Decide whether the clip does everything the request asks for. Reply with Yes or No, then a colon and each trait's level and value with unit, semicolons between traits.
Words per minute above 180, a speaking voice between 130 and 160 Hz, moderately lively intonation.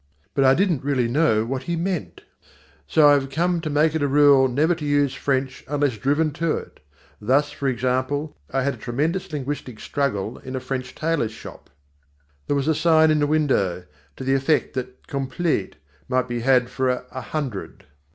Yes: average, 190 wpm; medium, 140 Hz; average, 3.0 semitones